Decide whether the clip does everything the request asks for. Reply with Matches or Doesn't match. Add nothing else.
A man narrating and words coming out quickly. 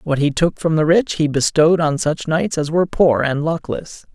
Matches